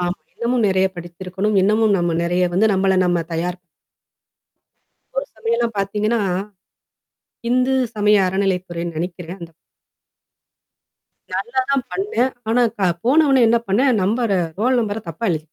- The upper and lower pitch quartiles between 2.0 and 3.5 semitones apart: No, average, 4.7 semitones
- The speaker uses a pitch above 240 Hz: No, high, 200 Hz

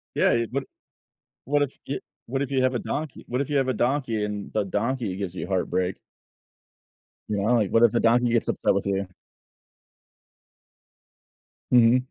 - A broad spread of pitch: No, average, 4.2 semitones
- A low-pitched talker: Yes, low, 120 Hz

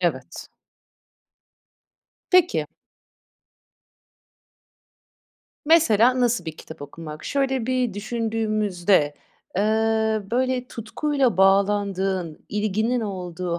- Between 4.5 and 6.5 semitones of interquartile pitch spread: Yes, average, 5.3 semitones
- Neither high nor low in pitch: No, high, 210 Hz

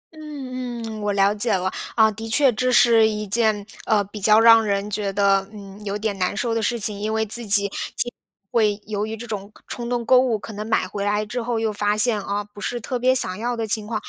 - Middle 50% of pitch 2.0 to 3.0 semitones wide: Yes, narrow, 2.4 semitones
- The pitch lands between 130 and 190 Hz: No, high, 215 Hz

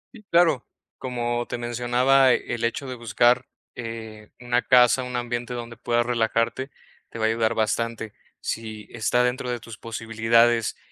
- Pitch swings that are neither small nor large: No, narrow, 1.4 semitones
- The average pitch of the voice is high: No, low, 120 Hz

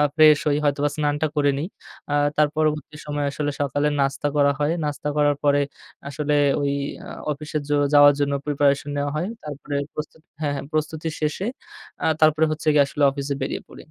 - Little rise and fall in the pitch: Yes, narrow, 1.1 semitones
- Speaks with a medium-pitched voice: Yes, medium, 145 Hz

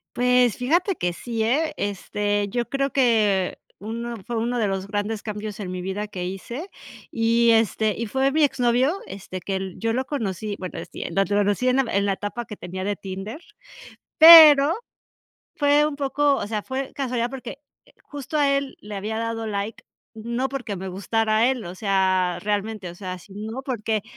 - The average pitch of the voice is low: No, high, 225 Hz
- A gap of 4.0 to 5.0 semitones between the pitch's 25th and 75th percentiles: Yes, average, 4.3 semitones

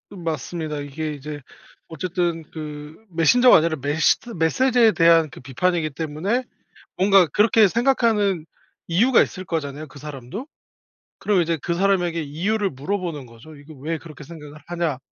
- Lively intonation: No, average, 4.4 semitones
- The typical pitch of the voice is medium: Yes, medium, 165 Hz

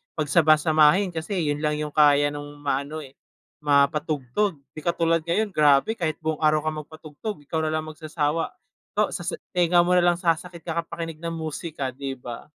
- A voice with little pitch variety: Yes, narrow, 2.3 semitones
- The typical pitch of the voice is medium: Yes, medium, 155 Hz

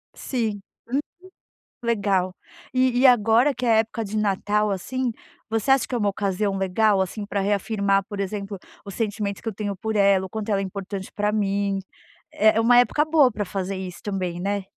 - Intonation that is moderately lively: No, narrow, 2.3 semitones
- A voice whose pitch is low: No, high, 205 Hz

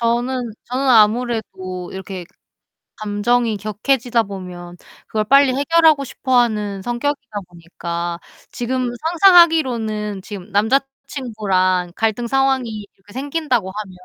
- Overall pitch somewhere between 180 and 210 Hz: No, high, 225 Hz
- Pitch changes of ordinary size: Yes, average, 4.7 semitones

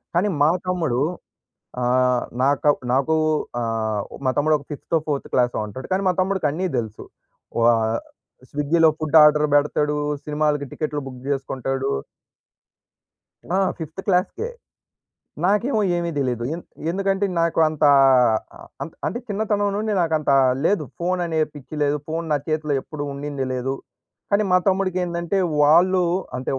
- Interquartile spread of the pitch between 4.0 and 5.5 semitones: Yes, average, 4.8 semitones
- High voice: No, medium, 155 Hz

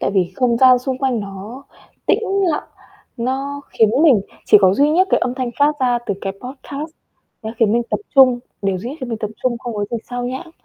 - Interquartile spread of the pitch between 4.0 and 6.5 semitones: No, average, 3.6 semitones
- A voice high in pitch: Yes, high, 245 Hz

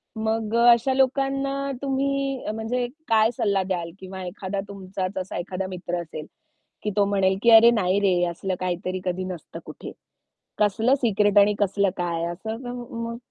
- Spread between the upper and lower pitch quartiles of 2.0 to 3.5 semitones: No, average, 4.0 semitones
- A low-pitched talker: No, high, 205 Hz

